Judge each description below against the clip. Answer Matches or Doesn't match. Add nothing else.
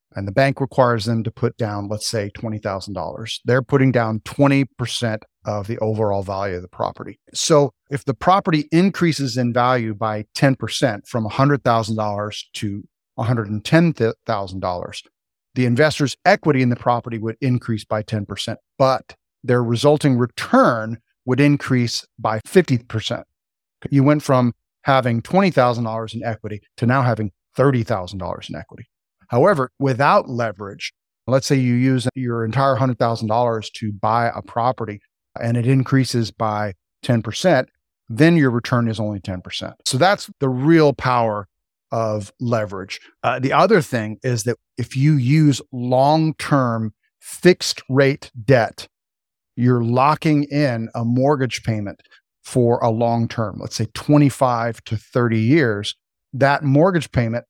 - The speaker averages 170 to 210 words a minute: Doesn't match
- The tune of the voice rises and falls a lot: Doesn't match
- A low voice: Matches